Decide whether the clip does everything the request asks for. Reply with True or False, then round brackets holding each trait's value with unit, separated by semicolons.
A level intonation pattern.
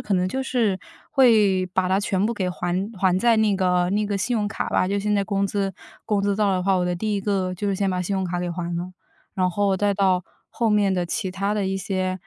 True (2.0 semitones)